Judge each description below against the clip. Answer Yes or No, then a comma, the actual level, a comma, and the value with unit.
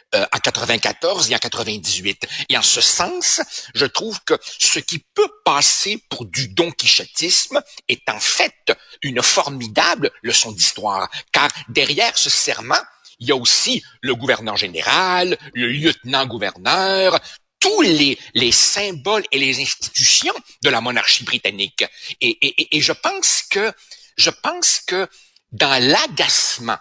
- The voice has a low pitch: No, medium, 160 Hz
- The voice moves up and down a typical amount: No, wide, 8.8 semitones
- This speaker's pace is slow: Yes, slow, 140 wpm